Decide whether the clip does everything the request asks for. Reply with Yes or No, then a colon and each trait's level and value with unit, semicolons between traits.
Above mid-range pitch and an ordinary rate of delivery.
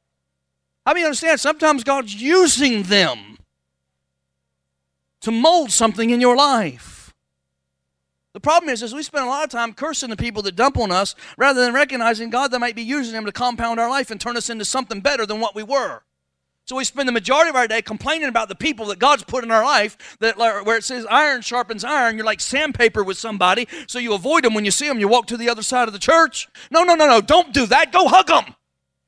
No: high, 235 Hz; fast, 225 wpm